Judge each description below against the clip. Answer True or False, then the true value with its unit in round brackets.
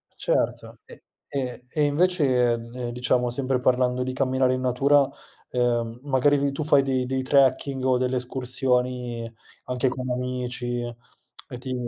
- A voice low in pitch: True (125 Hz)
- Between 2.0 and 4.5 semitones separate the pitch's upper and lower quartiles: False (1.4 semitones)